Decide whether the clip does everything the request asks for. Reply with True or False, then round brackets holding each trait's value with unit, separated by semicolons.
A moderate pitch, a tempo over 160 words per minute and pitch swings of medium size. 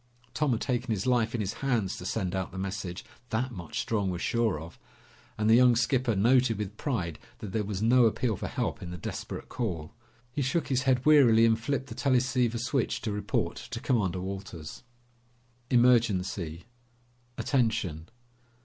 False (115 Hz; 175 wpm; 4.7 semitones)